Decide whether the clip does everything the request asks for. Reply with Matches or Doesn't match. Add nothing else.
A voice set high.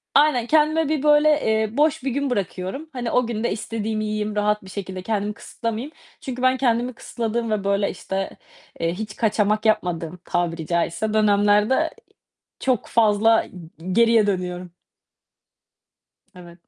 Matches